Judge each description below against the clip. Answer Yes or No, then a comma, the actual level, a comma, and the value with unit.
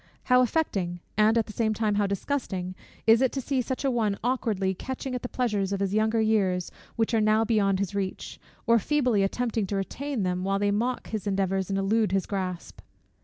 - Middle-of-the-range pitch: No, high, 215 Hz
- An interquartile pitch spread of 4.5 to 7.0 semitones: No, average, 3.4 semitones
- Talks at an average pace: No, fast, 210 wpm